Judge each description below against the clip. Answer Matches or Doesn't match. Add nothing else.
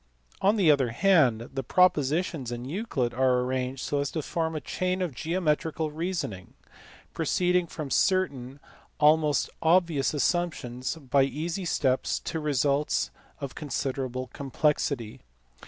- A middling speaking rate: Doesn't match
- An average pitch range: Matches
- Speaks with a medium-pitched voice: Matches